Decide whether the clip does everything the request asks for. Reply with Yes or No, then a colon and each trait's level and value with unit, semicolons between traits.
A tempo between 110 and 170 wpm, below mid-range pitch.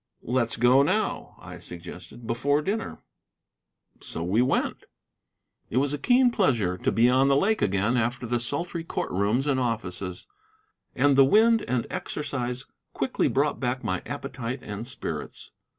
Yes: average, 150 wpm; low, 125 Hz